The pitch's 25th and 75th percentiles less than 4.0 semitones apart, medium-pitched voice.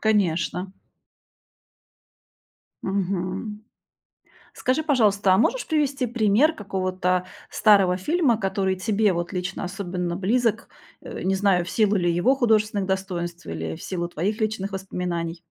No: average, 3.2 semitones; high, 195 Hz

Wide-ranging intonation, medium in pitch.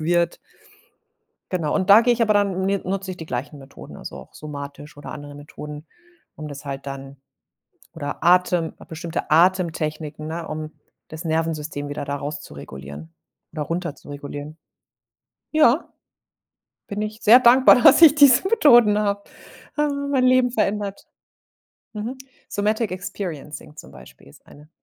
Yes: wide, 6.1 semitones; medium, 170 Hz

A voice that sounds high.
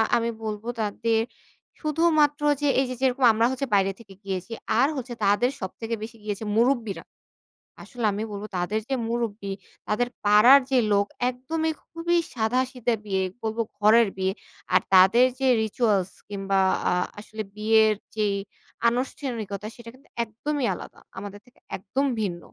Yes: high, 225 Hz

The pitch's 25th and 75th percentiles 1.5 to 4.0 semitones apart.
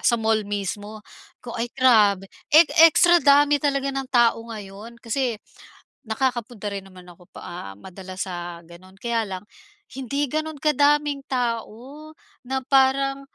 No: average, 5.2 semitones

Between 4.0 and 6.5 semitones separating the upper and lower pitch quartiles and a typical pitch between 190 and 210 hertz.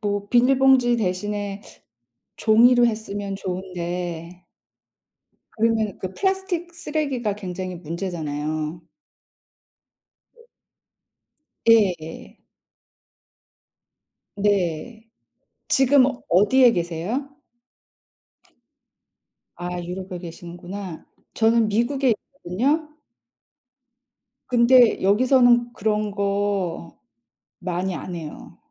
Yes: average, 5.2 semitones; high, 205 Hz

